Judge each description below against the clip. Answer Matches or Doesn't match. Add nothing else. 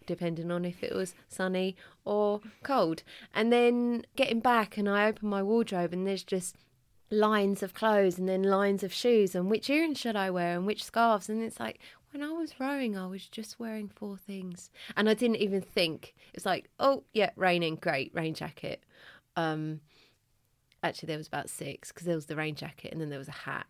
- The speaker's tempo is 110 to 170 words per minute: Doesn't match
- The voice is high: Matches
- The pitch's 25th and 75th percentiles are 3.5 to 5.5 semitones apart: Matches